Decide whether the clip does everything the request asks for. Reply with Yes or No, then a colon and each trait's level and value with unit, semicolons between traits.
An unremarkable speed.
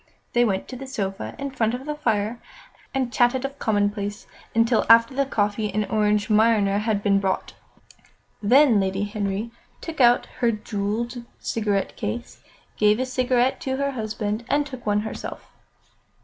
Yes: average, 160 wpm